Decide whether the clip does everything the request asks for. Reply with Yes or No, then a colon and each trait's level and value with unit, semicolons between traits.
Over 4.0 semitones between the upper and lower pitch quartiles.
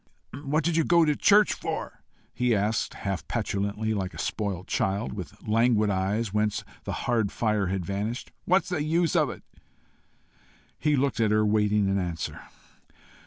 Yes: wide, 5.5 semitones